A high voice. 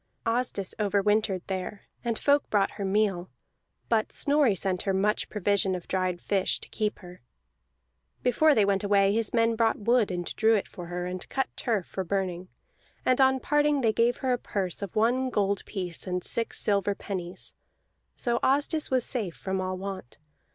Yes: high, 205 Hz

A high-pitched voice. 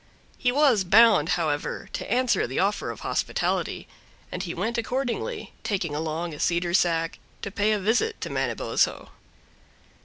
Yes: high, 200 Hz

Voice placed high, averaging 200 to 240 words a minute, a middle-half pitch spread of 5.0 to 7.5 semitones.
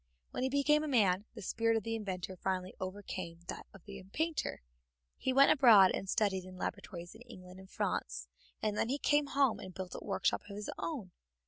Yes: high, 205 Hz; fast, 205 wpm; wide, 5.5 semitones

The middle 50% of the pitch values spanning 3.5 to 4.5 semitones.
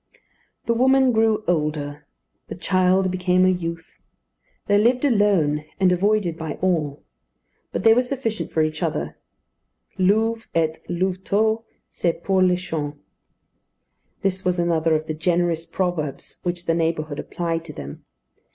Yes: average, 4.0 semitones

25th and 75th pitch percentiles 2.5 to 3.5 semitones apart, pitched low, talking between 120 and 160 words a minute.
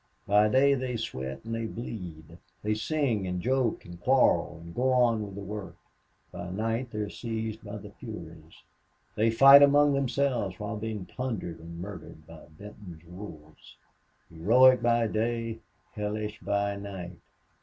No: average, 4.8 semitones; low, 105 Hz; average, 155 wpm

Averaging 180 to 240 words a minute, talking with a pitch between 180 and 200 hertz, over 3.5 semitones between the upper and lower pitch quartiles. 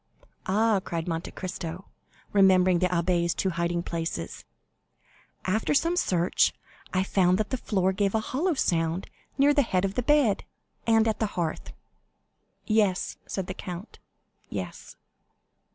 No: average, 140 wpm; high, 190 Hz; average, 4.0 semitones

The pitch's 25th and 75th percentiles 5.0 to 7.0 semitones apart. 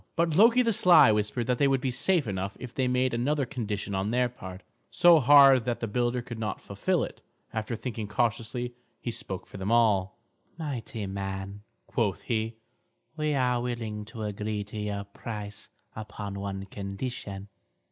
No: average, 3.7 semitones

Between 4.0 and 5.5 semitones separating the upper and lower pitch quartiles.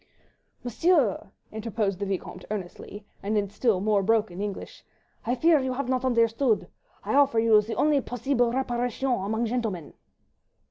No: average, 3.6 semitones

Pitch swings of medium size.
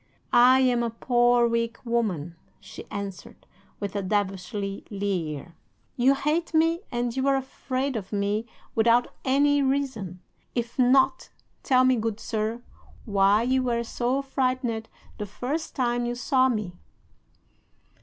Yes: average, 4.0 semitones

